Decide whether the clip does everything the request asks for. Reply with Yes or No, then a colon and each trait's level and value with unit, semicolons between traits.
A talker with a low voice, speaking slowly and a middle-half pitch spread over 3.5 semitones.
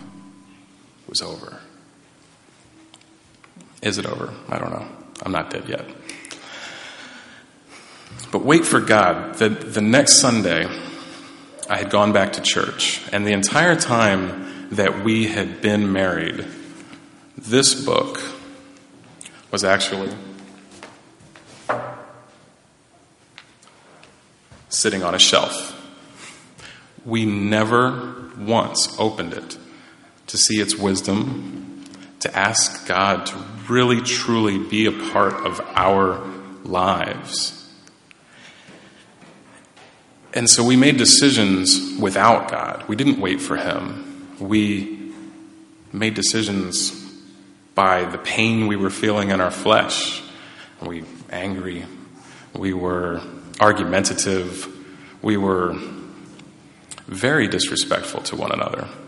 No: low, 100 Hz; slow, 105 wpm; average, 3.0 semitones